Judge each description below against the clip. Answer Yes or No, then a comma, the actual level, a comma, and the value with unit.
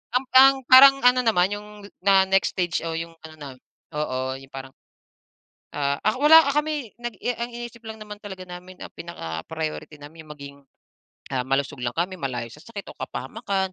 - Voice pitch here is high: No, medium, 180 Hz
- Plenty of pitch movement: Yes, wide, 7.7 semitones